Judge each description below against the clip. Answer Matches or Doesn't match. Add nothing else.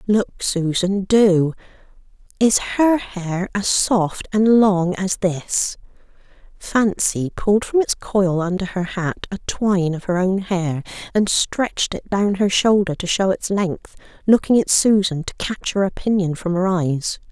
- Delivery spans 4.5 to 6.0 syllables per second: Doesn't match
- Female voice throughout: Matches